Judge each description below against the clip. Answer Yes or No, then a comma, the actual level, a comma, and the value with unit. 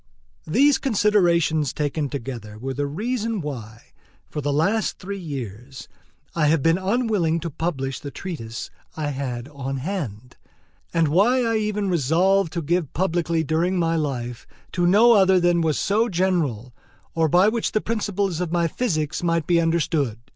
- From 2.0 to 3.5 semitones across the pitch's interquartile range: No, average, 5.3 semitones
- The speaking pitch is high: No, medium, 165 Hz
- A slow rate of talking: No, average, 160 wpm